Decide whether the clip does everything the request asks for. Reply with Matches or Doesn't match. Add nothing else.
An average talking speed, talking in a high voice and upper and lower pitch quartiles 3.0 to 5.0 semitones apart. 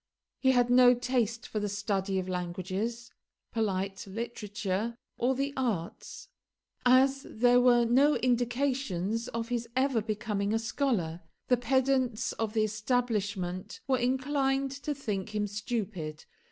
Doesn't match